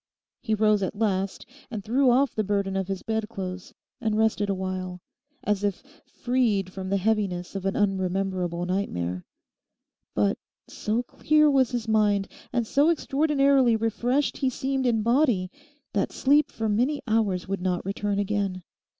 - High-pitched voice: Yes, high, 210 Hz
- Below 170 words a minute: Yes, average, 150 wpm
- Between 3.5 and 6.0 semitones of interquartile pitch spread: Yes, average, 4.2 semitones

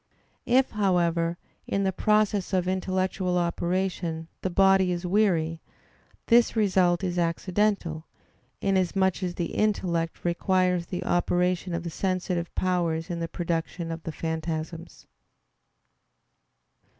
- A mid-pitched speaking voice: Yes, medium, 180 Hz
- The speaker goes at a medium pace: No, slow, 115 wpm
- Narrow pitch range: Yes, narrow, 2.0 semitones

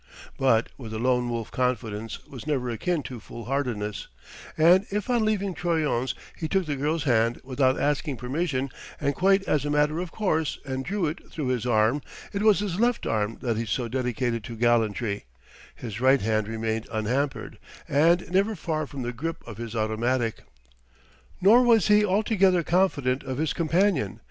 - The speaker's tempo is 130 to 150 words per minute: No, average, 175 wpm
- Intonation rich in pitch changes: Yes, wide, 6.7 semitones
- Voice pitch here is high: No, low, 135 Hz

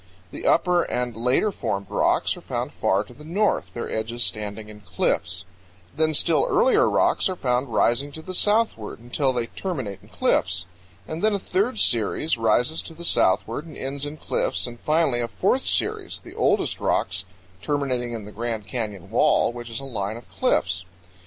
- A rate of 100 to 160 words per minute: No, average, 185 wpm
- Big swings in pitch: Yes, wide, 6.5 semitones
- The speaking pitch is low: Yes, low, 120 Hz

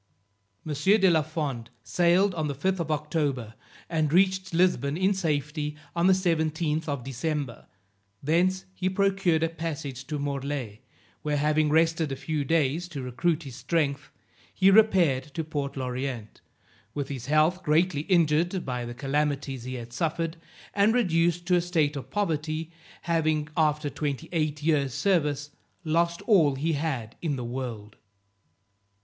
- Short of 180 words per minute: Yes, average, 150 wpm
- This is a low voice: No, medium, 155 Hz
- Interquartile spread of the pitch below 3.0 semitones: No, average, 3.4 semitones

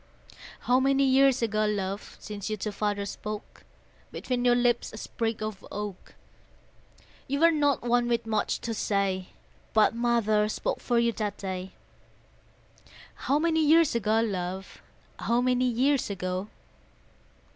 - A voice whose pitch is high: Yes, high, 225 Hz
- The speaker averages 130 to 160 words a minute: Yes, average, 140 wpm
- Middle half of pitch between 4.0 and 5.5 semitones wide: No, average, 3.4 semitones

